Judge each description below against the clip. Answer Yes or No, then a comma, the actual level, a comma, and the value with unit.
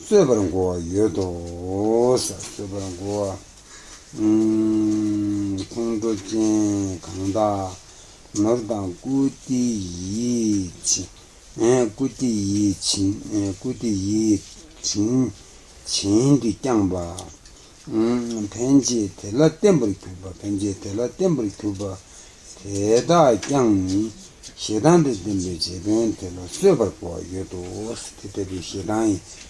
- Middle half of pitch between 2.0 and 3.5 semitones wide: Yes, average, 3.0 semitones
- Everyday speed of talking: No, slow, 80 wpm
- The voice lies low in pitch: Yes, low, 100 Hz